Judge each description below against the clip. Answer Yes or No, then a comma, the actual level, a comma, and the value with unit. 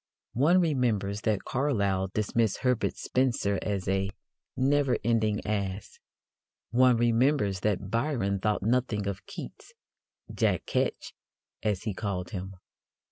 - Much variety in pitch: No, average, 4.3 semitones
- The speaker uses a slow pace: Yes, slow, 120 wpm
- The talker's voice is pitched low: Yes, low, 105 Hz